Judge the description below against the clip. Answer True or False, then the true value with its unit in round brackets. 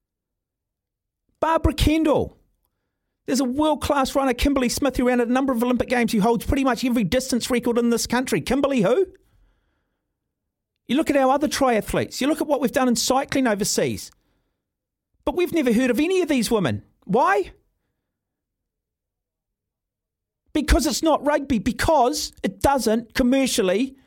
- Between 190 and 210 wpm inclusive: False (155 wpm)